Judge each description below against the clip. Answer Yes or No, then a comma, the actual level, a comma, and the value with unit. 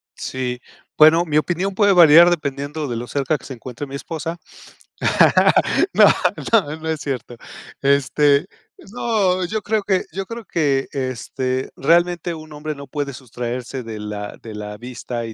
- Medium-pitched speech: Yes, medium, 145 Hz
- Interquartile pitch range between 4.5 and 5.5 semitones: Yes, average, 5.1 semitones